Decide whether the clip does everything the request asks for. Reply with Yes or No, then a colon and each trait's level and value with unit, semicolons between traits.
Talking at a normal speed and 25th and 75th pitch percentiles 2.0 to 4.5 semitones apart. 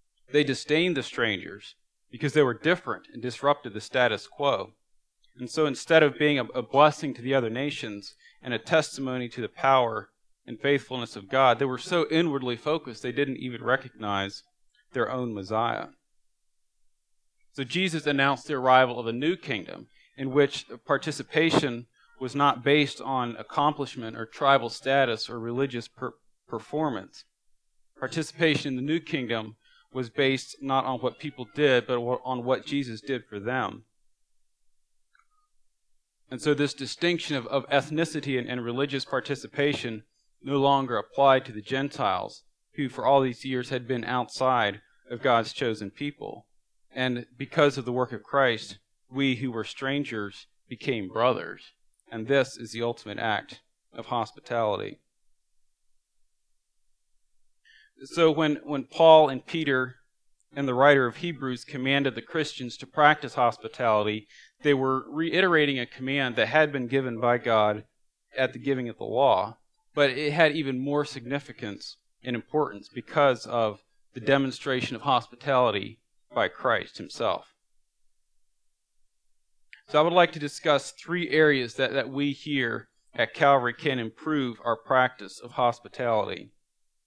Yes: average, 145 wpm; average, 3.0 semitones